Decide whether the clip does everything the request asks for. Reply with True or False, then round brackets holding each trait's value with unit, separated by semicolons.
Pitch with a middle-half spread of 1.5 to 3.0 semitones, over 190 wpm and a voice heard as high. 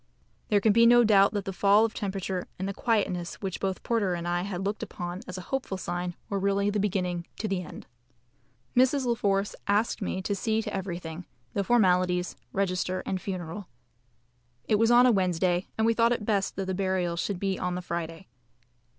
True (2.7 semitones; 200 wpm; 195 Hz)